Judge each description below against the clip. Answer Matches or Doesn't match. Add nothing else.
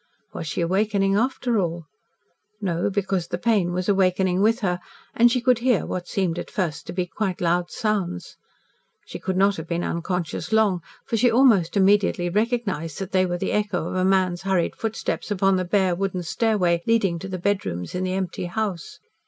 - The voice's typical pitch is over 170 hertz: Matches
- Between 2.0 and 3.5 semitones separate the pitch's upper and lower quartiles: Matches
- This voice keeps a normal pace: Matches